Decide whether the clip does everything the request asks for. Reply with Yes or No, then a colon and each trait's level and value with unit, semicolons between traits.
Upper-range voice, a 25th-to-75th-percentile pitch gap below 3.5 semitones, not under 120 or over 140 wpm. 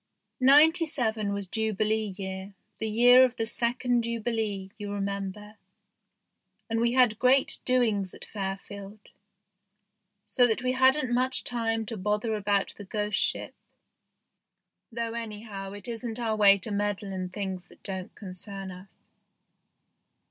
Yes: high, 215 Hz; average, 3.1 semitones; slow, 135 wpm